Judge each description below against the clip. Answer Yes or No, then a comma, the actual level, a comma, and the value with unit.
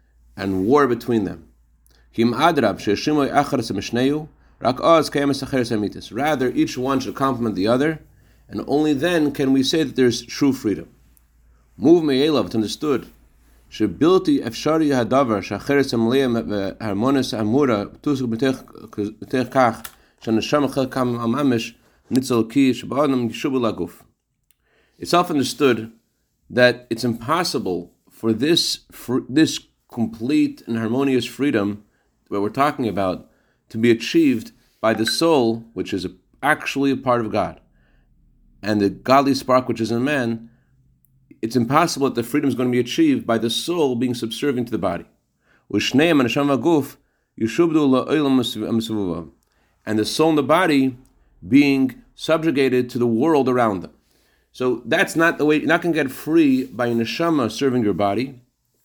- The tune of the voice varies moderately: Yes, average, 3.9 semitones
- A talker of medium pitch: No, low, 125 Hz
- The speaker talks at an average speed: No, slow, 110 wpm